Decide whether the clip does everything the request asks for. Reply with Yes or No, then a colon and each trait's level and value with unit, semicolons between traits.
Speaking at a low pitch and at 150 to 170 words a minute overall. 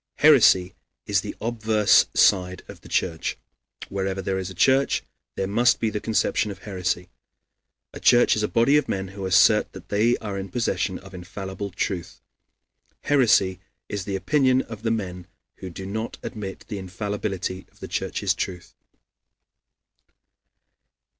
Yes: low, 100 Hz; average, 155 wpm